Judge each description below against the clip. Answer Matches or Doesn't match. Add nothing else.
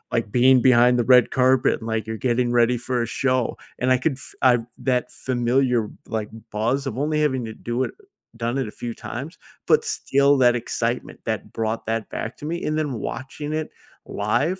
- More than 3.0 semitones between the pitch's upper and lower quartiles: Doesn't match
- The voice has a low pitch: Matches